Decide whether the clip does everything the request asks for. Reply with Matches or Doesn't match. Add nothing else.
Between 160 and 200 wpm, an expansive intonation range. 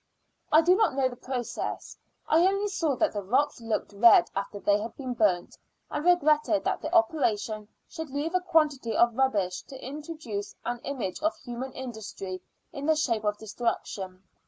Matches